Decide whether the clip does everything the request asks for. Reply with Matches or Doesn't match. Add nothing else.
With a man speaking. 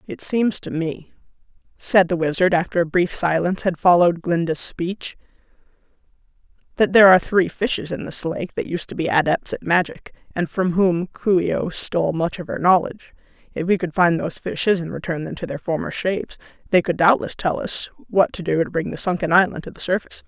Doesn't match